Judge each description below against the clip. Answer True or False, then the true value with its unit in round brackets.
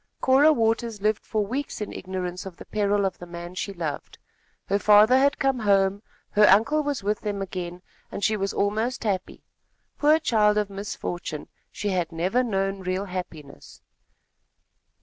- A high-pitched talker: True (200 Hz)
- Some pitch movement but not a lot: True (3.2 semitones)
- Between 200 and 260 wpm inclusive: False (165 wpm)